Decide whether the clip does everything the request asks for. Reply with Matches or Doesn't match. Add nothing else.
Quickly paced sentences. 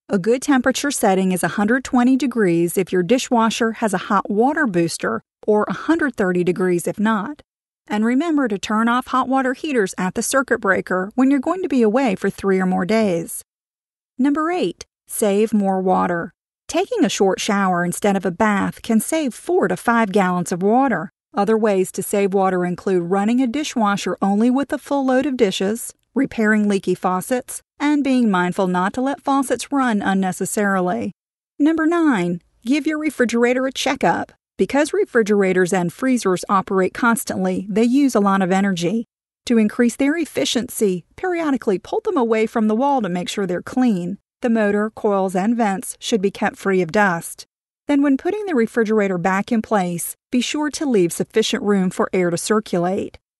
Doesn't match